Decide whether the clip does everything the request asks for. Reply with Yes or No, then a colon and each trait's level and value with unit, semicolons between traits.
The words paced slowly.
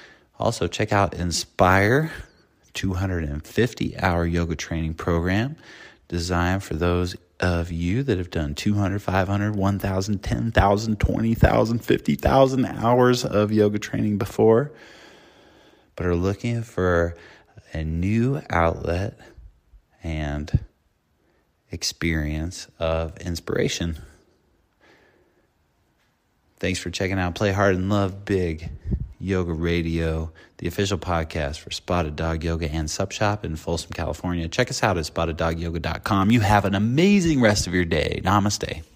Yes: slow, 120 wpm